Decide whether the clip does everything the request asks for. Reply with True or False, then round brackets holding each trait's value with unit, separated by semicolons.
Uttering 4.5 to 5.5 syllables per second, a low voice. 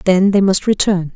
False (5.0 syllables/s; 190 Hz)